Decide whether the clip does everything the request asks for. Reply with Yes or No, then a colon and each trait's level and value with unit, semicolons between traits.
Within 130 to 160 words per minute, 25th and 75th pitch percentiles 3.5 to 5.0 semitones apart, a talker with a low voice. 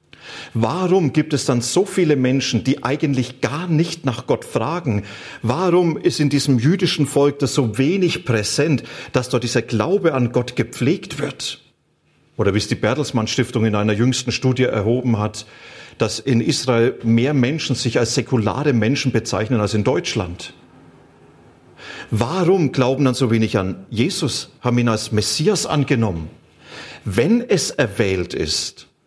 Yes: average, 150 wpm; average, 4.4 semitones; low, 130 Hz